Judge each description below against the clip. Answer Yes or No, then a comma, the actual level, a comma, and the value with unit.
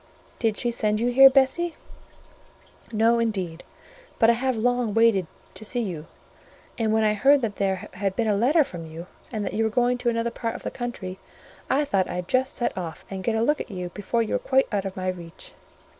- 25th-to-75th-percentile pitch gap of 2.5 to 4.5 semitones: Yes, average, 4.1 semitones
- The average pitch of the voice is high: Yes, high, 225 Hz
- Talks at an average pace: No, fast, 220 wpm